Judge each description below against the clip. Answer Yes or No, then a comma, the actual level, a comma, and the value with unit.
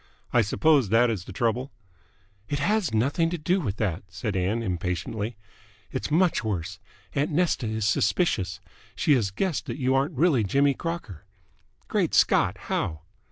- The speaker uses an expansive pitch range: Yes, wide, 7.1 semitones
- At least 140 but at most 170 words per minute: Yes, average, 155 wpm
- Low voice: Yes, low, 120 Hz